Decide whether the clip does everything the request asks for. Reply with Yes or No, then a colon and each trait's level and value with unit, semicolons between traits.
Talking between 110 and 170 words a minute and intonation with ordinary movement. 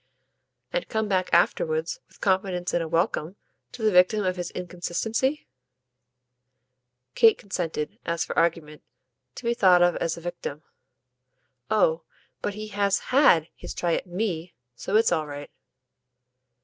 Yes: average, 145 wpm; average, 4.2 semitones